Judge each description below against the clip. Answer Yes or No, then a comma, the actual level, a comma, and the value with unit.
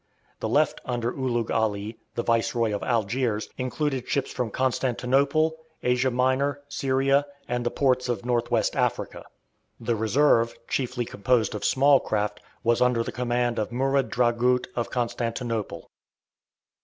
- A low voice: Yes, low, 125 Hz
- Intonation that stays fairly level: Yes, narrow, 2.1 semitones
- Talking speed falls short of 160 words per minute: Yes, average, 140 wpm